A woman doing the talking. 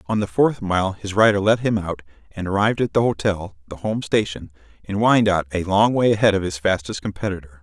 No: male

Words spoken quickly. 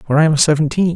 Yes: fast, 250 wpm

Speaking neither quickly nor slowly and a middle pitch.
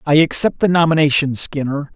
Yes: average, 155 wpm; medium, 150 Hz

